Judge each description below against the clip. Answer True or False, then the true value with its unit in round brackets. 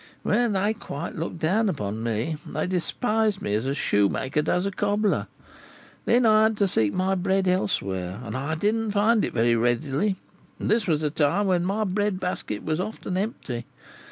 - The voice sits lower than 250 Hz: True (185 Hz)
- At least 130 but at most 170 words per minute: False (185 wpm)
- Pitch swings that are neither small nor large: False (7.4 semitones)